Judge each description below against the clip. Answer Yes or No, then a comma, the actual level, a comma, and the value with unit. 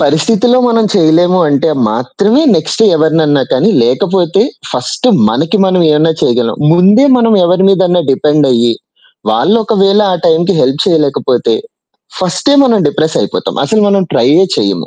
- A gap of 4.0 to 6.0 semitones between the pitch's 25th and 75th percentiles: Yes, average, 5.1 semitones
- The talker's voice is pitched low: No, medium, 175 Hz